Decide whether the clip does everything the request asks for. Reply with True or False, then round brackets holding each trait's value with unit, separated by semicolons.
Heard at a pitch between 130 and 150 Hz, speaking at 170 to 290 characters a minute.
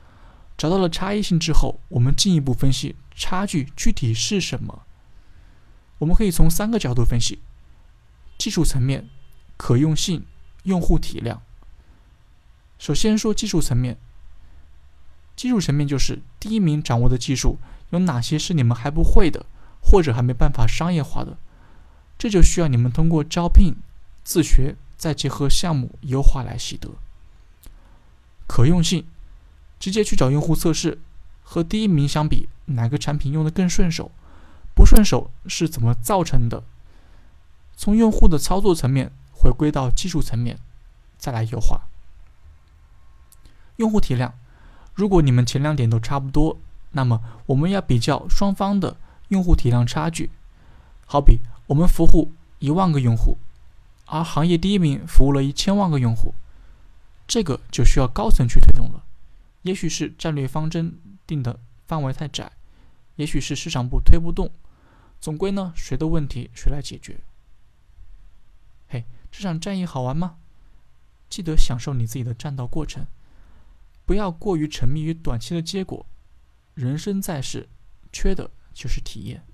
True (135 Hz; 230 characters per minute)